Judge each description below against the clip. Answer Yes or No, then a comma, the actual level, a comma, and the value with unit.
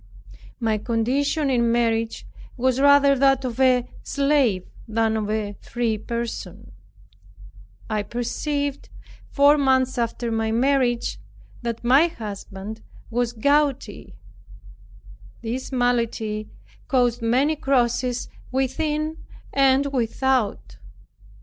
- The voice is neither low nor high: No, high, 245 Hz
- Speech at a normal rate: No, slow, 100 wpm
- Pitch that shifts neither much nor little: Yes, average, 3.3 semitones